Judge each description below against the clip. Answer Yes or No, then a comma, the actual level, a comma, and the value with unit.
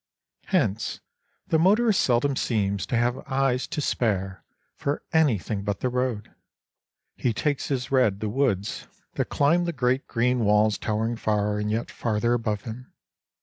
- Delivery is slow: No, average, 150 wpm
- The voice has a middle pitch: No, low, 120 Hz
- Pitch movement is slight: No, average, 4.3 semitones